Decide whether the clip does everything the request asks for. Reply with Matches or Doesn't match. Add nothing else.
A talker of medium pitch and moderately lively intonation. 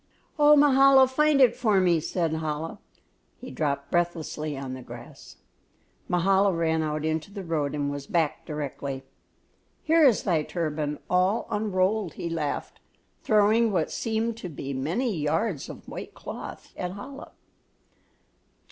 Doesn't match